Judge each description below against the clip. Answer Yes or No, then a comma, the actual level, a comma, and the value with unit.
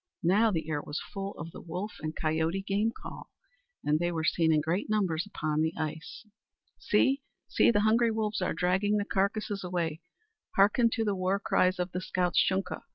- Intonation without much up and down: No, average, 4.2 semitones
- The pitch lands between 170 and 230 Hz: Yes, medium, 185 Hz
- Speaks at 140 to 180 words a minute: No, average, 190 wpm